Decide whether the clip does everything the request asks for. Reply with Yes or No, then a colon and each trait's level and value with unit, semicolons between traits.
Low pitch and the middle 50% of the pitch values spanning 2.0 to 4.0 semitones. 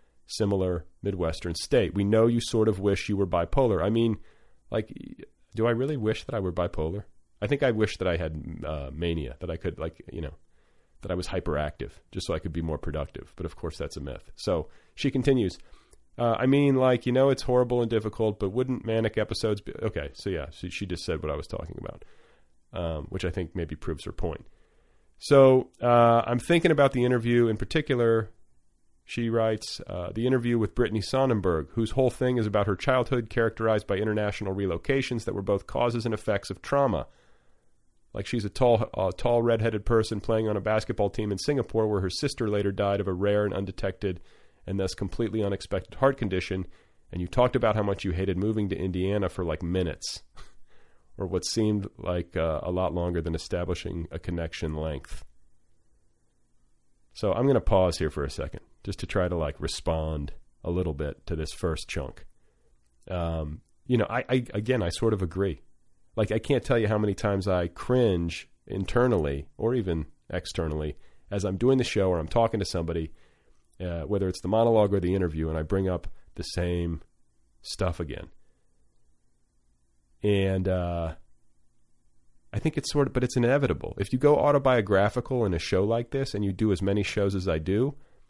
No: low, 100 Hz; average, 5.1 semitones